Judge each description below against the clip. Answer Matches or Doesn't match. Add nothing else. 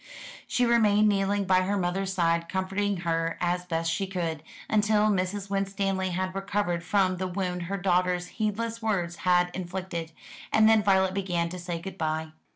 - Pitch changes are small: Matches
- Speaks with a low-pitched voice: Doesn't match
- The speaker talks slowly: Doesn't match